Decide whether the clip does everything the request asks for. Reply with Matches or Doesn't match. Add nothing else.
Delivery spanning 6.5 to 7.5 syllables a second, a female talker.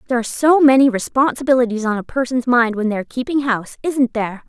Matches